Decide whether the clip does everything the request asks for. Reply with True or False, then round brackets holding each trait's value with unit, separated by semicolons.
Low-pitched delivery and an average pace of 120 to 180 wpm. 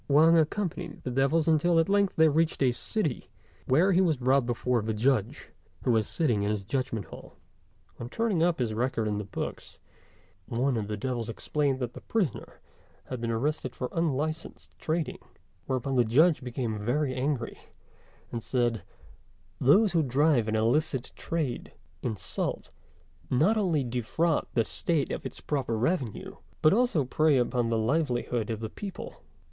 True (130 Hz; 165 wpm)